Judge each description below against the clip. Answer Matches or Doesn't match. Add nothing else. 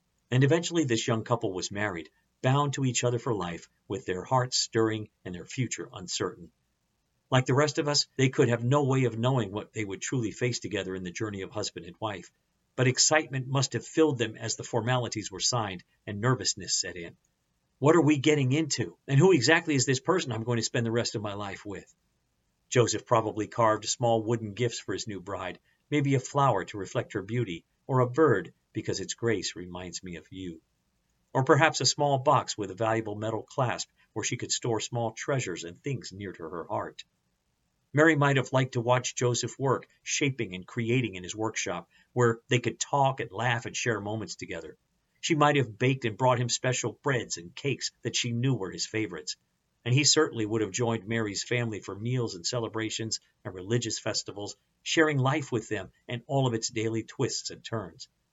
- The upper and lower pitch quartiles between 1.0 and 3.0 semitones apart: Doesn't match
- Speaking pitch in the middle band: Doesn't match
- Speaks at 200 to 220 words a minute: Matches